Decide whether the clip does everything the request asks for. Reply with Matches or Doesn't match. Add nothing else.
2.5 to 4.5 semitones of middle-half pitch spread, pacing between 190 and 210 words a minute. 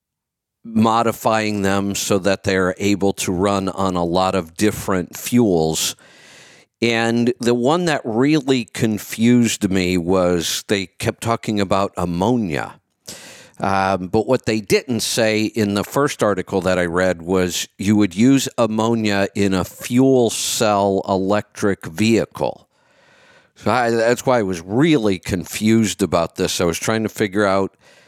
Doesn't match